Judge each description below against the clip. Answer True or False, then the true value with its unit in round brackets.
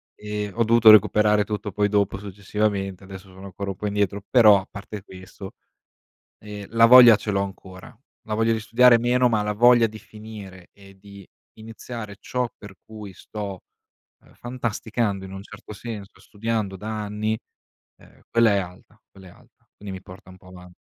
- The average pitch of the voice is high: False (105 Hz)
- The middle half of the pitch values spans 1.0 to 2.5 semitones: True (2.2 semitones)